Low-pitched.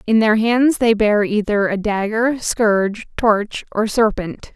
No: high, 215 Hz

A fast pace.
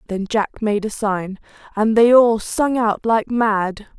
No: average, 180 wpm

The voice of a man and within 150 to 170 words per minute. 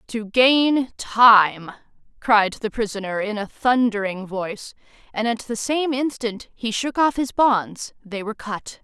No: female; average, 155 wpm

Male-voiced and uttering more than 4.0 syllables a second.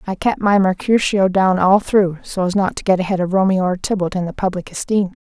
No: female; 5.4 syllables/s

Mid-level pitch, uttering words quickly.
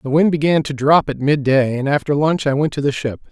Yes: medium, 145 Hz; fast, 270 wpm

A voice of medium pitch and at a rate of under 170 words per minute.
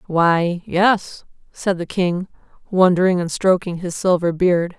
Yes: medium, 180 Hz; average, 140 wpm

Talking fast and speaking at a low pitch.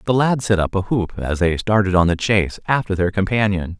Yes: fast, 235 wpm; low, 100 Hz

